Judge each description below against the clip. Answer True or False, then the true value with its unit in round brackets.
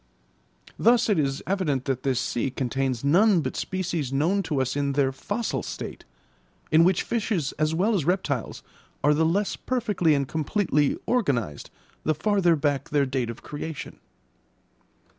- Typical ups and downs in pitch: False (5.8 semitones)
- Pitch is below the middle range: False (155 Hz)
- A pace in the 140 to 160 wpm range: True (155 wpm)